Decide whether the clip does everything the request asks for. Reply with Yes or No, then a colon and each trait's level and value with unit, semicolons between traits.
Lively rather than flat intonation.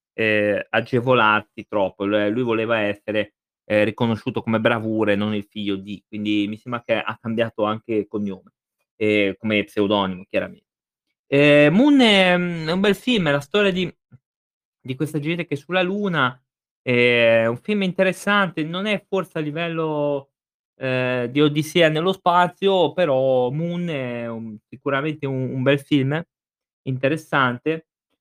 Yes: wide, 6.8 semitones